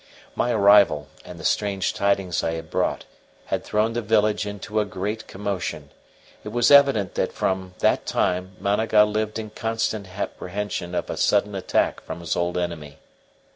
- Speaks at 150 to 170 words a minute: Yes, average, 165 wpm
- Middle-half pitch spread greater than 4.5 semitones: No, average, 2.9 semitones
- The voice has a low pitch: Yes, low, 100 Hz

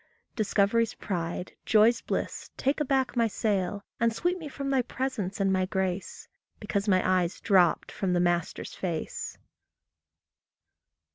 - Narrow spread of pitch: No, average, 4.1 semitones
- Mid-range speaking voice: No, high, 200 Hz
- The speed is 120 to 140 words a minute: Yes, slow, 135 wpm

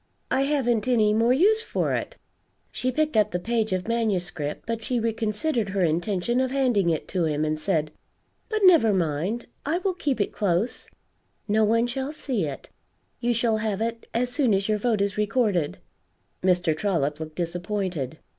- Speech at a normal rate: Yes, average, 175 wpm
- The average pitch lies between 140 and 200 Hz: No, high, 215 Hz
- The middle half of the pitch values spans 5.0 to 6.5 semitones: Yes, wide, 5.5 semitones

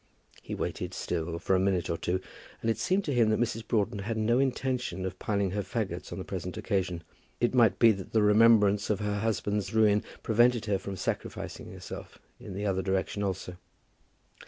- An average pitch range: Yes, average, 3.0 semitones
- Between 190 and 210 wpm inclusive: Yes, average, 195 wpm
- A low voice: Yes, low, 105 Hz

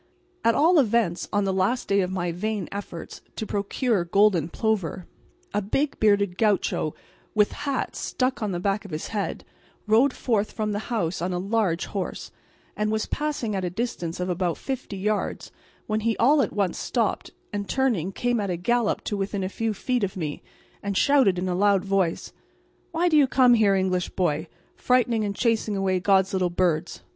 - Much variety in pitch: No, average, 3.6 semitones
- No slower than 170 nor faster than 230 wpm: Yes, average, 190 wpm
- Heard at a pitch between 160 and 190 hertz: No, high, 205 Hz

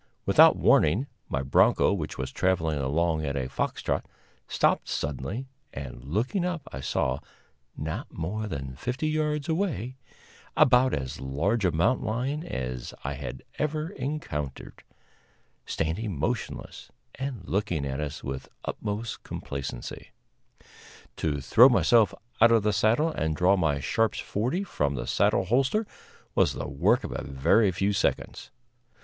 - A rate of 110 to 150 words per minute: Yes, average, 145 wpm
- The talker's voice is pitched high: No, very low, 95 Hz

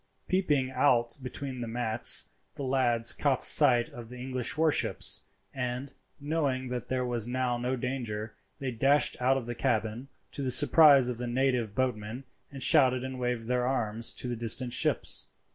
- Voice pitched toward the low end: Yes, low, 125 Hz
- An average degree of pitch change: No, narrow, 1.9 semitones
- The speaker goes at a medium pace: Yes, average, 170 wpm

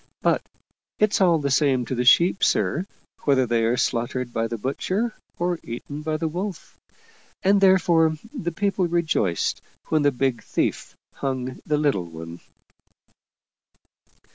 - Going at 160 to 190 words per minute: No, average, 140 wpm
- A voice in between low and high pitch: Yes, medium, 145 Hz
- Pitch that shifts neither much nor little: No, wide, 5.9 semitones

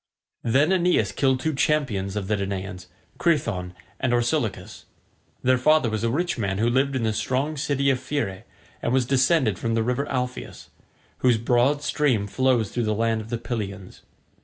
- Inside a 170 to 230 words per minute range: Yes, average, 175 wpm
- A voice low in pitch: Yes, low, 120 Hz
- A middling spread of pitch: Yes, average, 4.2 semitones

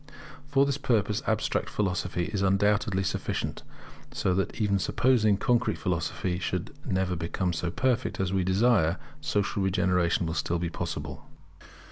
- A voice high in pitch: No, very low, 95 Hz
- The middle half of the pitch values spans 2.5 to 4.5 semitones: Yes, average, 2.9 semitones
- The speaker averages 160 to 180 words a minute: No, average, 145 wpm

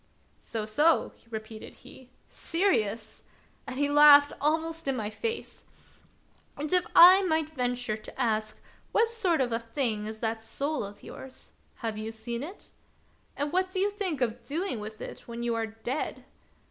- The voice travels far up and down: Yes, wide, 6.4 semitones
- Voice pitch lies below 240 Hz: No, very high, 255 Hz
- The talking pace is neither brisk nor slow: Yes, average, 185 wpm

